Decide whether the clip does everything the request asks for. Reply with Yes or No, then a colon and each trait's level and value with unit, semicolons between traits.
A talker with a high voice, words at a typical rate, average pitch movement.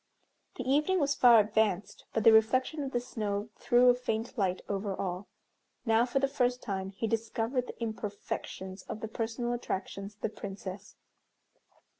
Yes: high, 225 Hz; average, 165 wpm; average, 3.5 semitones